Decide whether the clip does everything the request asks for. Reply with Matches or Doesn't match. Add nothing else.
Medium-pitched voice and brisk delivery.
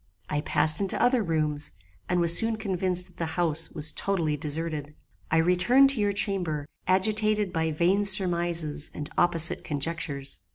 Doesn't match